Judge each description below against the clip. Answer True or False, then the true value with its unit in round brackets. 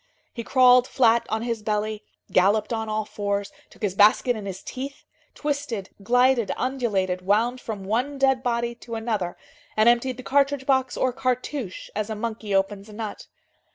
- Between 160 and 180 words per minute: True (170 wpm)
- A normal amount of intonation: True (3.4 semitones)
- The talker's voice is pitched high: True (230 Hz)